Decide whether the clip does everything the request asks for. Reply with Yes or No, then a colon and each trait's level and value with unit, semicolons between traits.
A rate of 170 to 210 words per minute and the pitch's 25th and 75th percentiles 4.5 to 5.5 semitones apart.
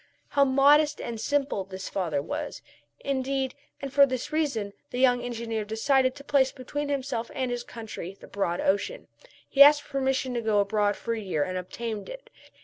Yes: average, 180 wpm; average, 4.8 semitones